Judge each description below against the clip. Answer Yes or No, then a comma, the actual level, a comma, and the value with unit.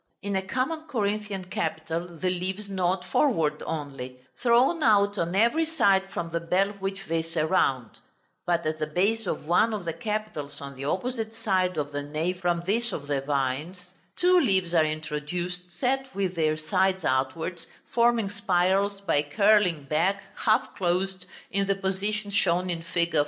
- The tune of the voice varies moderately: Yes, average, 3.9 semitones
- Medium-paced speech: Yes, average, 165 wpm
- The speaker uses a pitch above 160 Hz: Yes, medium, 185 Hz